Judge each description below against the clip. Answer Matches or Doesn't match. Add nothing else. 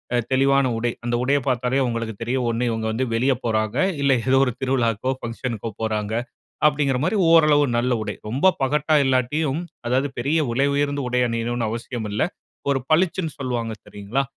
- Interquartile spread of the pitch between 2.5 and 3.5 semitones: Matches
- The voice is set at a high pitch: Doesn't match